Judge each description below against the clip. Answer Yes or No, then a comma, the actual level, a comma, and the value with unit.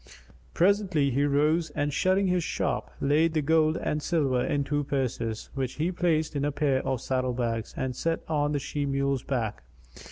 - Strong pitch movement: No, average, 3.1 semitones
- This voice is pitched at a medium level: Yes, medium, 145 Hz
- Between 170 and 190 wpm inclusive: Yes, average, 185 wpm